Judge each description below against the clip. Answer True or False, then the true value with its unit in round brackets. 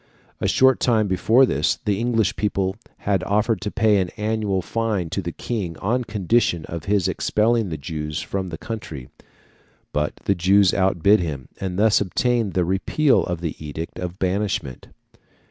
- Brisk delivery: False (165 wpm)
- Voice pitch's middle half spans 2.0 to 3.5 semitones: False (4.0 semitones)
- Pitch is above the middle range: False (100 Hz)